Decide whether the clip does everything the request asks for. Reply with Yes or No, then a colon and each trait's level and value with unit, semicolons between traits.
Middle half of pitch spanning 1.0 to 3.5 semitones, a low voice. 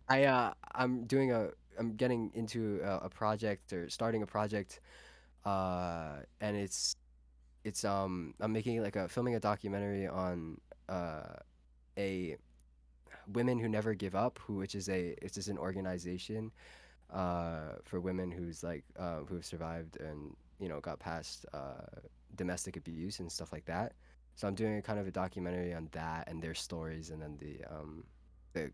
No: average, 4.5 semitones; very low, 90 Hz